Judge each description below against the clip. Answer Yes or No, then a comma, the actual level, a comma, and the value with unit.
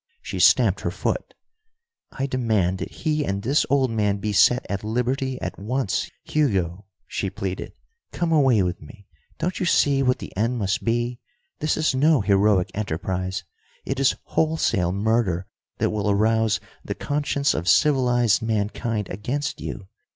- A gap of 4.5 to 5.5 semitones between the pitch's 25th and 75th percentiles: Yes, average, 5.2 semitones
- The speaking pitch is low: Yes, low, 110 Hz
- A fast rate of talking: No, average, 155 wpm